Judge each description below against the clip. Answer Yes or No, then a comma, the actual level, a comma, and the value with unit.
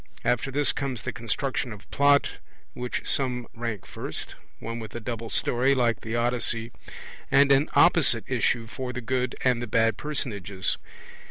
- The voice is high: No, low, 120 Hz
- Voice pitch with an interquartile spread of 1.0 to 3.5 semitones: Yes, narrow, 2.5 semitones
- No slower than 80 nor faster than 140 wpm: No, average, 160 wpm